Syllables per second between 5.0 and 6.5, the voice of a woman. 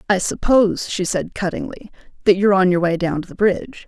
Yes: 6.0 syllables/s; female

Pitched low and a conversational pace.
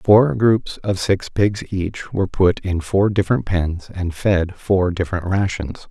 Yes: very low, 95 Hz; average, 175 wpm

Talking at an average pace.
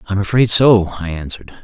Yes: average, 185 wpm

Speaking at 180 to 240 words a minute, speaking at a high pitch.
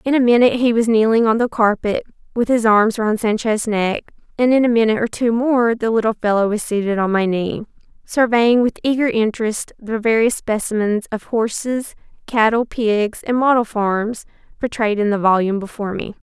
Yes: average, 185 wpm; high, 225 Hz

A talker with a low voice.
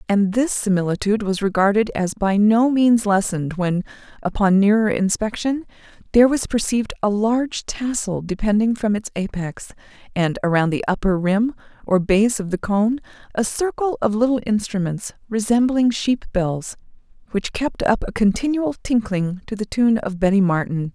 No: high, 210 Hz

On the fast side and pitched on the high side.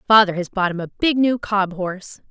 Yes: fast, 235 wpm; high, 200 Hz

